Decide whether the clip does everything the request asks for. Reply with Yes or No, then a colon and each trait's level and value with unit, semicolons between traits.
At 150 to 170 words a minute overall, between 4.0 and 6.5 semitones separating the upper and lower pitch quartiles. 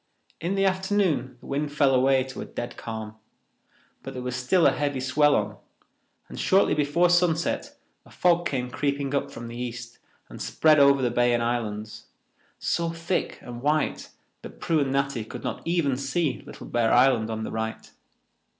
No: average, 180 wpm; average, 4.6 semitones